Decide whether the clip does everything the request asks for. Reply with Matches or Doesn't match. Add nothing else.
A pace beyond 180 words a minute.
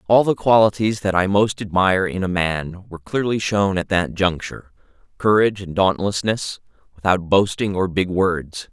Doesn't match